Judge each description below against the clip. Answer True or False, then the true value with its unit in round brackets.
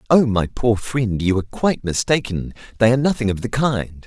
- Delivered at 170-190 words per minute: False (205 wpm)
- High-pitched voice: False (115 Hz)